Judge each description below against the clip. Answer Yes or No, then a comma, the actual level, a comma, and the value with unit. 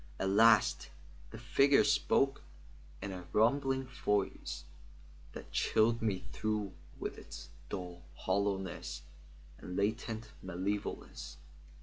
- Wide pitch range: No, average, 3.3 semitones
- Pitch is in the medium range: No, low, 105 Hz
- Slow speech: Yes, slow, 100 wpm